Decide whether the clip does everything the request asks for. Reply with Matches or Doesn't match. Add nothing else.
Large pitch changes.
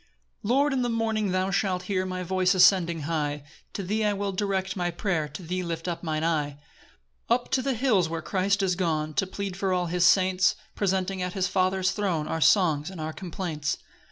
Doesn't match